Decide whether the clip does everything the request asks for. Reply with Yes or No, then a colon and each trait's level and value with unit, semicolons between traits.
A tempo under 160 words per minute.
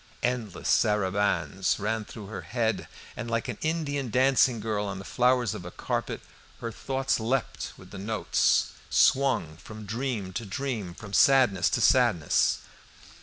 Yes: average, 150 wpm